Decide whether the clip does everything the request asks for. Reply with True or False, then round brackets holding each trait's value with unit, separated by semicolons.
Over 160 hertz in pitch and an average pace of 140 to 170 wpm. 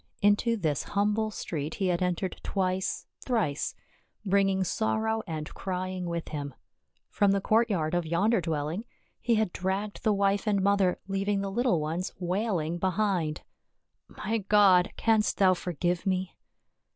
True (190 Hz; 145 wpm)